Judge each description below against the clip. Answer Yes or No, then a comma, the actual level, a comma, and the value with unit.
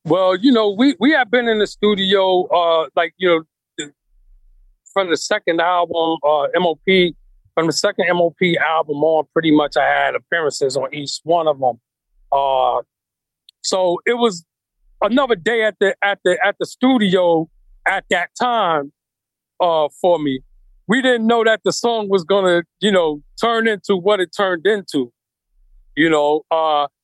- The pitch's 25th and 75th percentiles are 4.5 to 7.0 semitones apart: Yes, average, 5.2 semitones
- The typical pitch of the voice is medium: Yes, medium, 175 Hz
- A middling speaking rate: Yes, average, 165 wpm